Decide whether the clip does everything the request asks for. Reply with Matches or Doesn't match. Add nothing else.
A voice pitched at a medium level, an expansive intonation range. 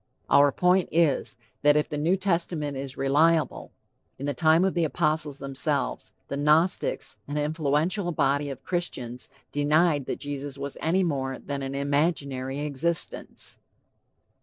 Doesn't match